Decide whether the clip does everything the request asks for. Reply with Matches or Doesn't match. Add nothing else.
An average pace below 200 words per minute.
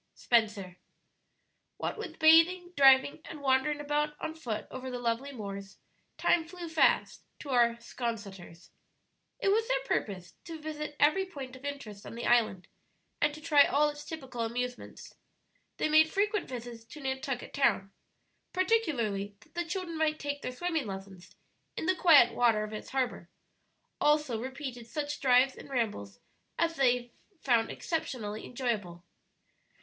Matches